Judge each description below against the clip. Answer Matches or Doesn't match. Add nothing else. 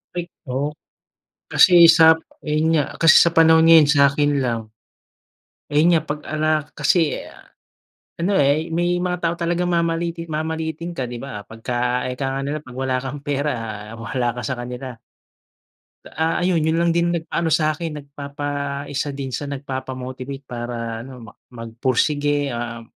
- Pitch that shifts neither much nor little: Matches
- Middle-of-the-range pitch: Matches